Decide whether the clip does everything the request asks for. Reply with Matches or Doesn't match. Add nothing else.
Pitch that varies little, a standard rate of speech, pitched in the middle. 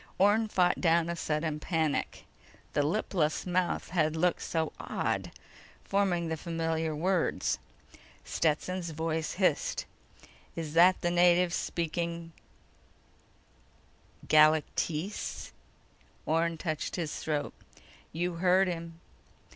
Doesn't match